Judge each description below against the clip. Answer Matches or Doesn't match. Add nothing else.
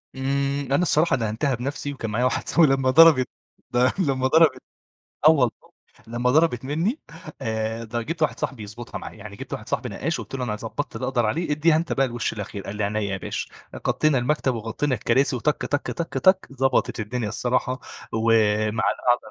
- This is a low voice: Matches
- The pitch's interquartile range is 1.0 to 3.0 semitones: Doesn't match